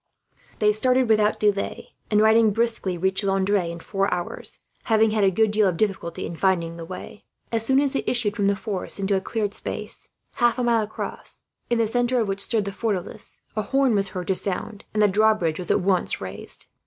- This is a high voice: Yes, high, 210 Hz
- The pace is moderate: No, fast, 215 wpm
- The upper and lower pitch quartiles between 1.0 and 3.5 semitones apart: Yes, average, 2.8 semitones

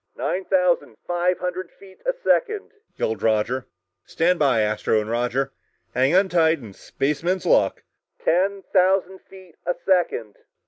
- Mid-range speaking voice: Yes, medium, 175 Hz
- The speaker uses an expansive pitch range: Yes, wide, 6.9 semitones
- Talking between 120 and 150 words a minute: Yes, slow, 135 wpm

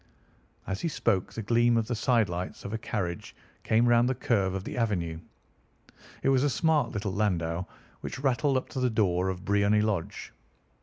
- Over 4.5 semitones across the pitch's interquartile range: No, average, 4.2 semitones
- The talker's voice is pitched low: Yes, low, 110 Hz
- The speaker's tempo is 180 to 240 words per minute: Yes, average, 185 wpm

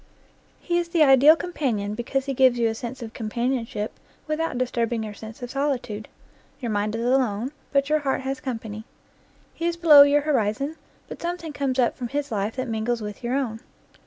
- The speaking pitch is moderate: No, very high, 255 Hz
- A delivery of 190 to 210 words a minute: Yes, average, 195 wpm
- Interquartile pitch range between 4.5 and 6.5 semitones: No, average, 4.1 semitones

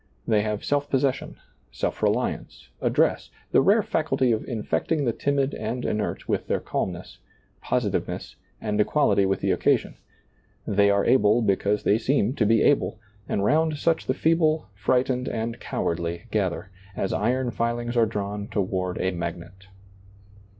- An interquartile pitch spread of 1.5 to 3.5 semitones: No, average, 4.5 semitones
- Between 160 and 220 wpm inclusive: No, average, 150 wpm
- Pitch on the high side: No, low, 110 Hz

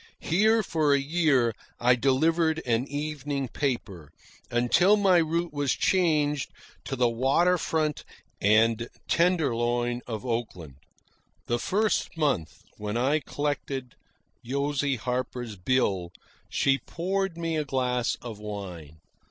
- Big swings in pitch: No, average, 5.0 semitones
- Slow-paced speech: Yes, slow, 120 wpm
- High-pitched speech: No, low, 135 Hz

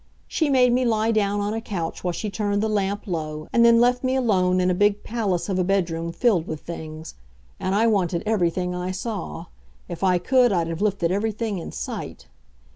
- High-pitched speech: Yes, high, 200 Hz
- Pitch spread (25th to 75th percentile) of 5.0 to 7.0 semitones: No, average, 4.0 semitones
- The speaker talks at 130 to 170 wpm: No, fast, 205 wpm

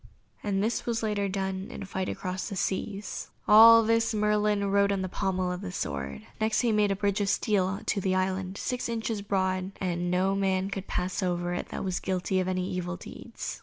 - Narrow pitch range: Yes, narrow, 2.0 semitones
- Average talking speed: No, fast, 210 wpm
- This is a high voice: Yes, high, 195 Hz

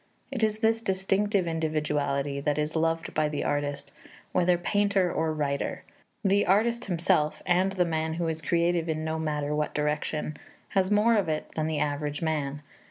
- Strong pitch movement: No, average, 4.1 semitones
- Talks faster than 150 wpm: Yes, average, 170 wpm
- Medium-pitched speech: Yes, medium, 160 Hz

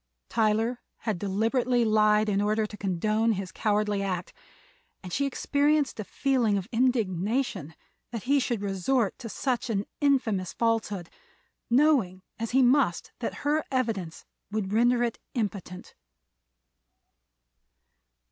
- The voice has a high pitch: Yes, high, 220 Hz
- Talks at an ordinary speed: No, slow, 125 wpm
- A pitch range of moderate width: Yes, average, 3.9 semitones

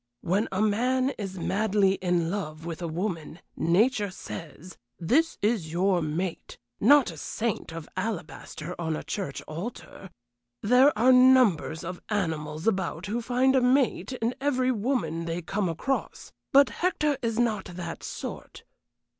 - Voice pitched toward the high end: Yes, high, 195 Hz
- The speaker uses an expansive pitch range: Yes, wide, 6.7 semitones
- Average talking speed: Yes, average, 145 wpm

